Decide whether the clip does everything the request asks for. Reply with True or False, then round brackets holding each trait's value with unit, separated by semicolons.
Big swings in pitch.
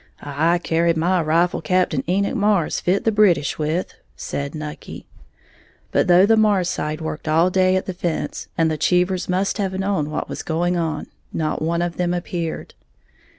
False (2.7 semitones)